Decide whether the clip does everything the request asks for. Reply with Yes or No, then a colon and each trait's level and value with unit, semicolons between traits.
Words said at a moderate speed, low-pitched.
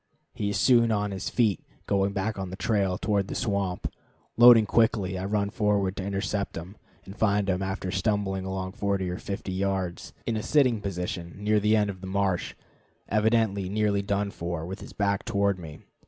Yes: average, 190 wpm; low, 100 Hz